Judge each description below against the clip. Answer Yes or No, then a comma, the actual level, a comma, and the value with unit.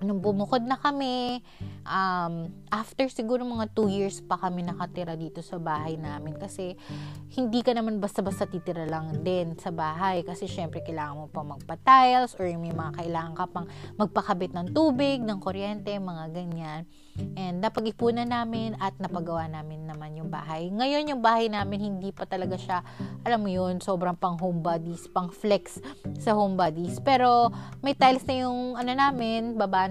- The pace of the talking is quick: No, average, 165 wpm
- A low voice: No, medium, 185 Hz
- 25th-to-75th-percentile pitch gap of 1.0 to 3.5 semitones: No, average, 5.2 semitones